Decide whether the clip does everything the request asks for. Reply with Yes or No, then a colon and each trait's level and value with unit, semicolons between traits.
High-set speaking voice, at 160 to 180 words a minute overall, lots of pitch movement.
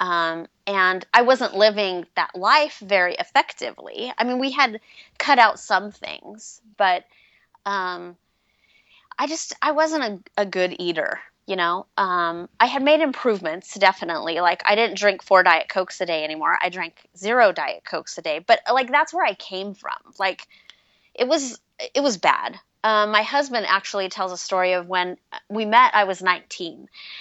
Yes: high, 205 Hz; average, 175 wpm; wide, 6.3 semitones